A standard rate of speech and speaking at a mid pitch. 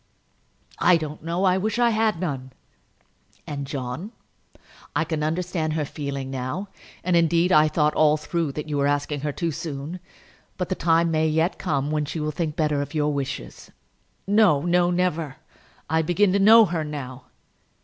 Yes: average, 180 wpm; medium, 155 Hz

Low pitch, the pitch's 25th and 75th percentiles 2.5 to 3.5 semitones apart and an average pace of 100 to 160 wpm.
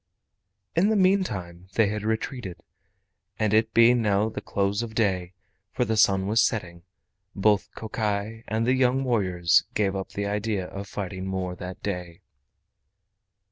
Yes: low, 105 Hz; average, 3.0 semitones; average, 150 wpm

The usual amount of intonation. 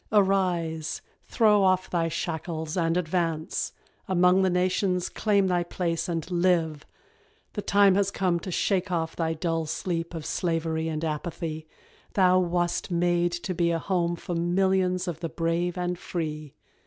No: narrow, 2.0 semitones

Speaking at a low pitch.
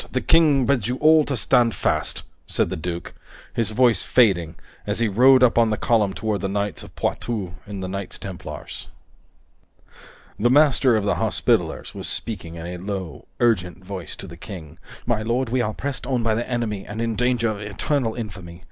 Yes: low, 110 Hz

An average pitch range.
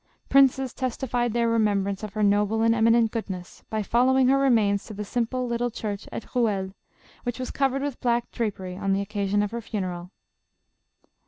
Yes: average, 3.2 semitones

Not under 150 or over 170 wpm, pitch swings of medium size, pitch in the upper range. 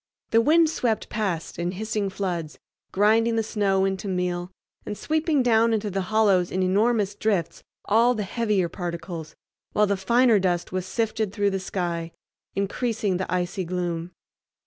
Yes: average, 155 wpm; average, 3.5 semitones; high, 200 Hz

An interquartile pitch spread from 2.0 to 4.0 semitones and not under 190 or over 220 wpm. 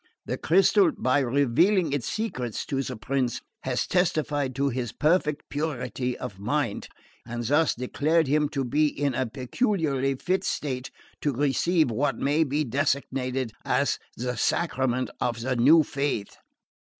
No: average, 3.3 semitones; average, 145 wpm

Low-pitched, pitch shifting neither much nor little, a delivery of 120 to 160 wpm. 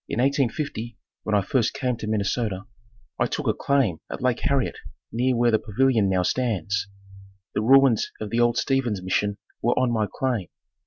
No: low, 115 Hz; average, 3.8 semitones; average, 175 wpm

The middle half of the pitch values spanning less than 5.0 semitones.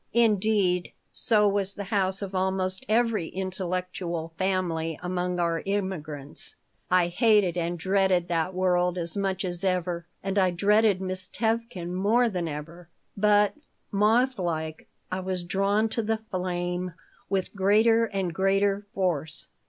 Yes: narrow, 2.5 semitones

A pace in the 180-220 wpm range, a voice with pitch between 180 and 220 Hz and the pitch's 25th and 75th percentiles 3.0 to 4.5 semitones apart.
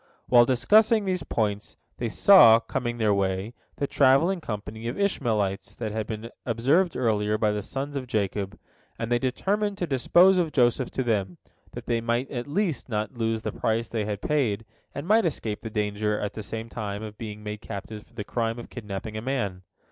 No: average, 195 wpm; low, 115 Hz; average, 4.1 semitones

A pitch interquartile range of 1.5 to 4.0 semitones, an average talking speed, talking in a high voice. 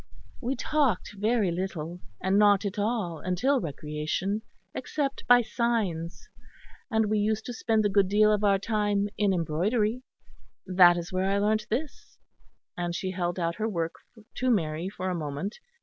Yes: average, 3.7 semitones; average, 160 wpm; high, 200 Hz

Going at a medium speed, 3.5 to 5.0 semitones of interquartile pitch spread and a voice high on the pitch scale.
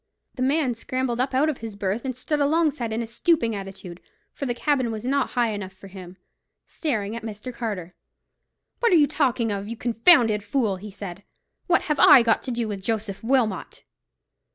Yes: average, 190 wpm; average, 4.5 semitones; high, 230 Hz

